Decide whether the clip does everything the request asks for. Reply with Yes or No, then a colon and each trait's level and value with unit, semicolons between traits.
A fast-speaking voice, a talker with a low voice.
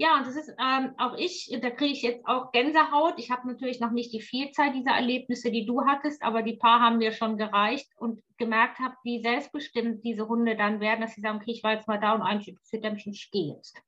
No: fast, 240 wpm; high, 235 Hz